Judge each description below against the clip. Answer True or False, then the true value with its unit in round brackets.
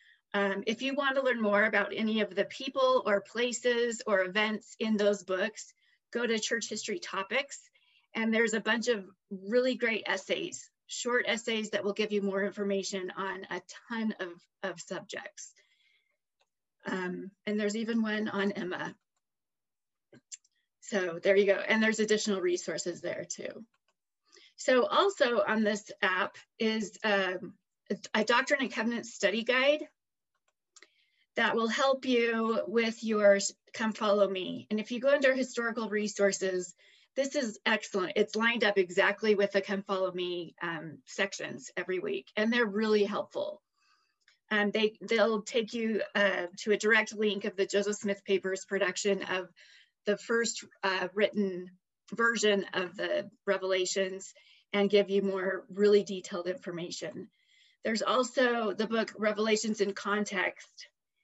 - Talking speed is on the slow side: False (150 wpm)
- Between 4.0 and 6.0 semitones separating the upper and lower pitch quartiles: False (2.9 semitones)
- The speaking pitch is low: False (210 Hz)